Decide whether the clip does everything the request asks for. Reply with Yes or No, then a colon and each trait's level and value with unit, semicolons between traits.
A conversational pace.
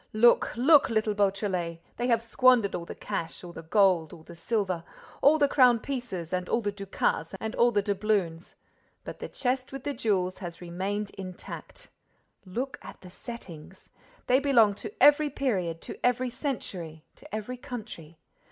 Yes: average, 170 wpm